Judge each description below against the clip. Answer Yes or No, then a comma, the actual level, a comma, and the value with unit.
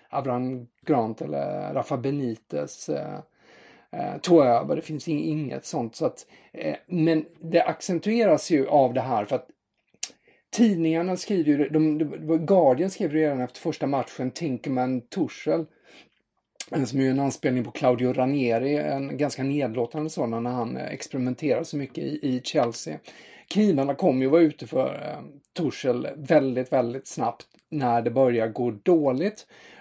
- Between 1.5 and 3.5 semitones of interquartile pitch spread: No, average, 4.1 semitones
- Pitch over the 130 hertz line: Yes, medium, 140 Hz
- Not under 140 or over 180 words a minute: Yes, average, 145 wpm